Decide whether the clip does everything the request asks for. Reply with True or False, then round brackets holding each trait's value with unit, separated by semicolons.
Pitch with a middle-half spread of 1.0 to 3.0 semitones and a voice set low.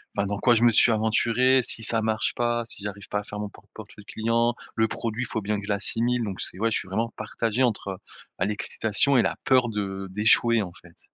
True (2.4 semitones; 110 Hz)